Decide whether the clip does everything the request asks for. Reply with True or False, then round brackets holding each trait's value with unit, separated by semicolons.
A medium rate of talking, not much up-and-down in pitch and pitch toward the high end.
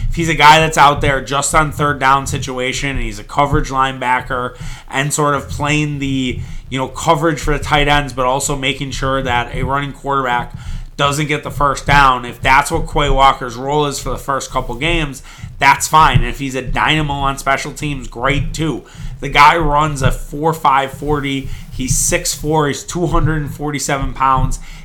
False (195 wpm; 2.2 semitones; 140 Hz)